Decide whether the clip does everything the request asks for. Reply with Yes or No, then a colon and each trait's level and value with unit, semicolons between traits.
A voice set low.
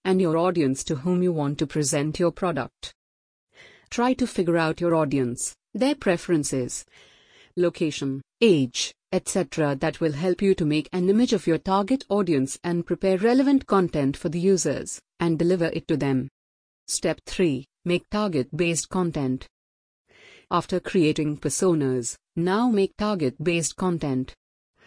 No: medium, 165 Hz